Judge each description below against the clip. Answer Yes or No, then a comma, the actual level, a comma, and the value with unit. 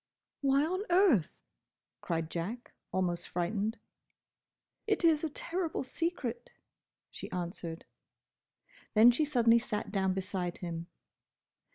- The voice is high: Yes, high, 225 Hz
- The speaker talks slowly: Yes, slow, 105 wpm